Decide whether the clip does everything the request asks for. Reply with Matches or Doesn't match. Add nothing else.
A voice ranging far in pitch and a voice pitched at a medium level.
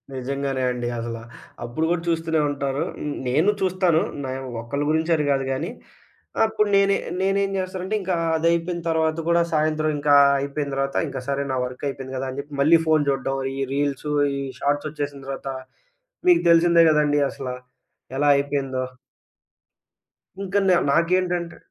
Doesn't match